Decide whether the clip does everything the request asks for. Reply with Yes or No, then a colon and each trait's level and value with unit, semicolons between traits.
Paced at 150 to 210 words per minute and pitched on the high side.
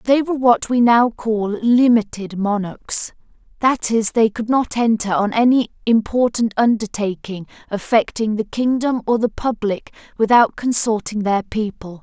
No: average, 140 wpm; high, 225 Hz